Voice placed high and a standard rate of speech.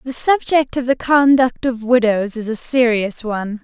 Yes: high, 240 Hz; average, 180 wpm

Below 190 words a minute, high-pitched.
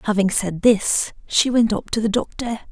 No: average, 200 wpm; high, 215 Hz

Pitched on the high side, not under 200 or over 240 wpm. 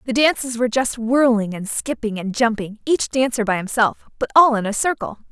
Yes: high, 235 Hz; fast, 205 wpm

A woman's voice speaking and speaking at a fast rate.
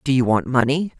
Yes: female; fast, 240 wpm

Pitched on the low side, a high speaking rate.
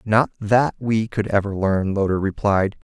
No: low, 105 Hz; average, 165 wpm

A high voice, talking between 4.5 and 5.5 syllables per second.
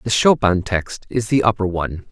No: low, 100 Hz; 5.1 syllables/s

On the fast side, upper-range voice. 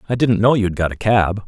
No: fast, 325 wpm; low, 105 Hz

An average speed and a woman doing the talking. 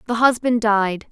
Yes: average, 160 wpm; female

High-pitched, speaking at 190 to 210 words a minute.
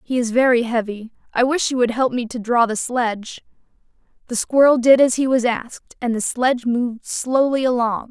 Yes: high, 245 Hz; average, 200 wpm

